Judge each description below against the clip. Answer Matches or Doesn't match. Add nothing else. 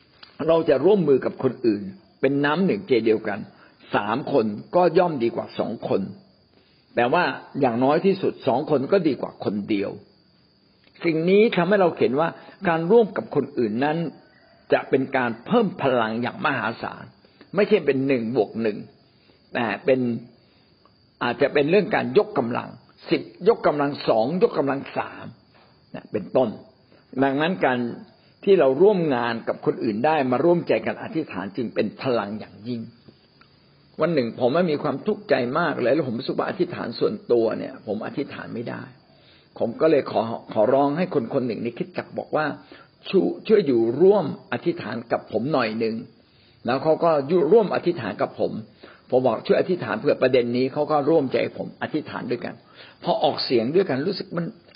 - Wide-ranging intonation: Matches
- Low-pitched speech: Doesn't match